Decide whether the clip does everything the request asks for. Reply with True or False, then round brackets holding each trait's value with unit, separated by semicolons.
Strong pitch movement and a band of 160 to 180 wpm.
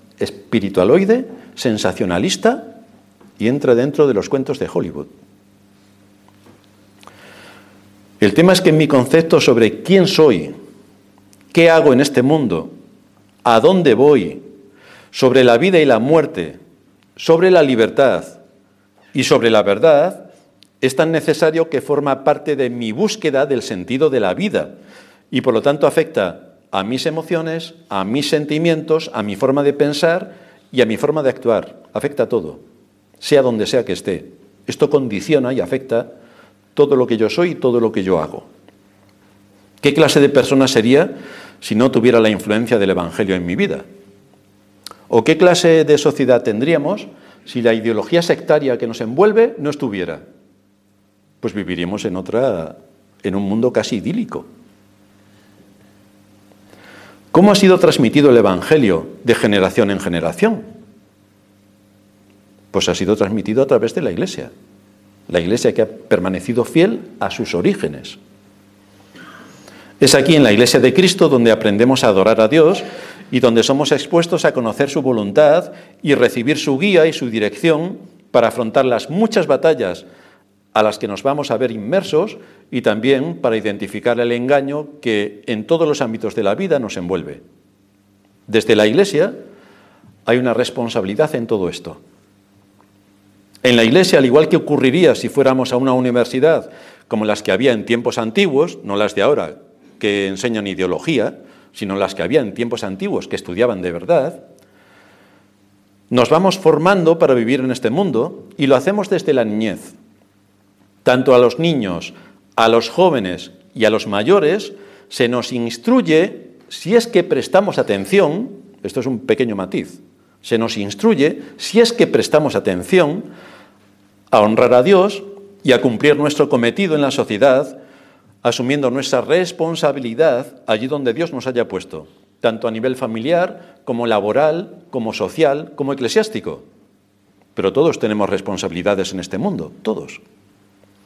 False (7.4 semitones; 150 wpm)